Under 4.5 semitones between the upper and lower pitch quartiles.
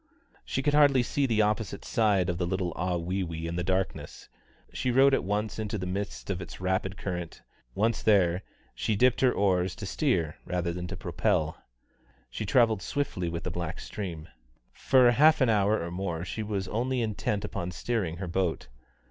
Yes: average, 4.0 semitones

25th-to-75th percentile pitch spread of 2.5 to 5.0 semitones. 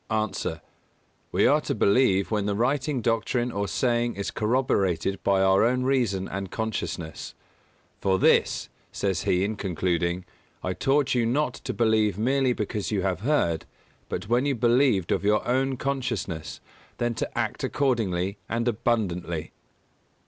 Yes: average, 4.4 semitones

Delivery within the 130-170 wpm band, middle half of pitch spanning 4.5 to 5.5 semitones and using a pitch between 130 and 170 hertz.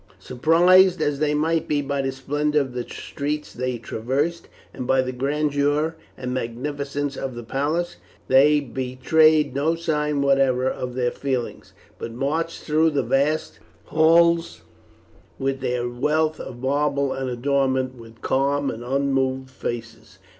No: average, 140 wpm; average, 2.7 semitones; medium, 140 Hz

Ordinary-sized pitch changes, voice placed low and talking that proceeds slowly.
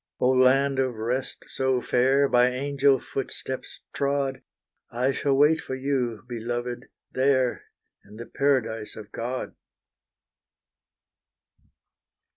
No: narrow, 2.1 semitones; low, 130 Hz; slow, 105 wpm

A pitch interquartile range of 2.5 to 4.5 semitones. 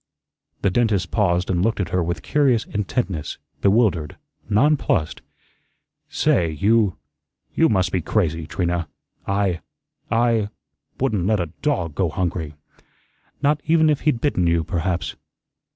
No: average, 5.0 semitones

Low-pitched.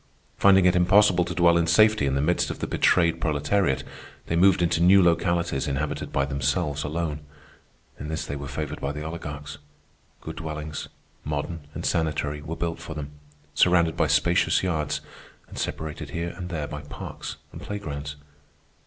Yes: very low, 80 Hz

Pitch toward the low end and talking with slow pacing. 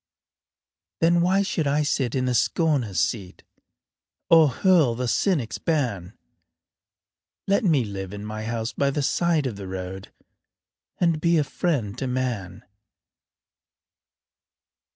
Yes: low, 130 Hz; slow, 130 wpm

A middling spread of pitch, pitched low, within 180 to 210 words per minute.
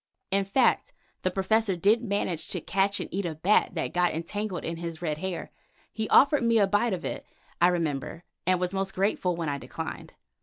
No: average, 3.1 semitones; high, 190 Hz; average, 200 wpm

